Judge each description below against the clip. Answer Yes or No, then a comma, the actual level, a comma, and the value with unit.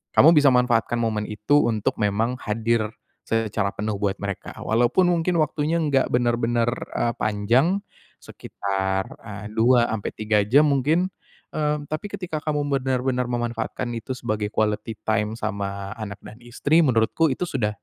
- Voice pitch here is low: Yes, low, 115 Hz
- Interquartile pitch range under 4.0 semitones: No, average, 4.7 semitones